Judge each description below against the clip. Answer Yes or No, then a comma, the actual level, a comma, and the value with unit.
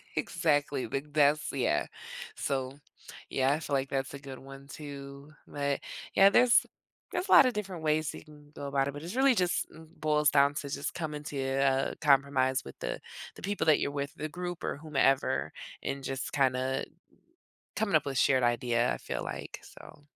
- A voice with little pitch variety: Yes, narrow, 2.3 semitones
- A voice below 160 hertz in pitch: Yes, medium, 140 Hz